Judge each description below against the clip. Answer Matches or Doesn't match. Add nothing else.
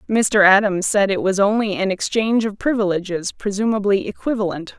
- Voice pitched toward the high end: Matches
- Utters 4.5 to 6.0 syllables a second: Matches